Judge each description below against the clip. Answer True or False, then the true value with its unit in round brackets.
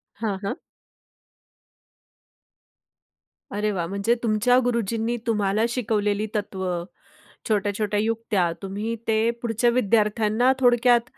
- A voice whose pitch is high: True (215 Hz)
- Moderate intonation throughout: False (2.3 semitones)